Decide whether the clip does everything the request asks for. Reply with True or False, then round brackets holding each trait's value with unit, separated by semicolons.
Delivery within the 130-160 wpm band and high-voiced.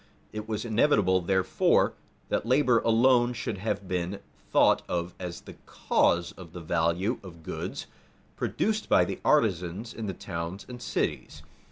False (150 wpm; 100 Hz)